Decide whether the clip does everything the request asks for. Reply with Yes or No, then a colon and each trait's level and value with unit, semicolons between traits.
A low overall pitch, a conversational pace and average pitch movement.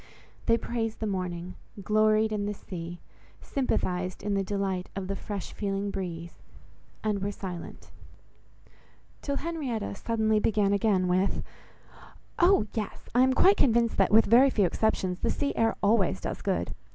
No: high, 205 Hz; average, 145 wpm; average, 3.2 semitones